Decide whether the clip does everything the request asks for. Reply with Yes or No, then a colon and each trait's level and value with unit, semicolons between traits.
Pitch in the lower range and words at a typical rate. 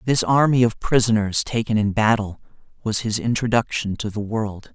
Yes: low, 110 Hz; average, 165 wpm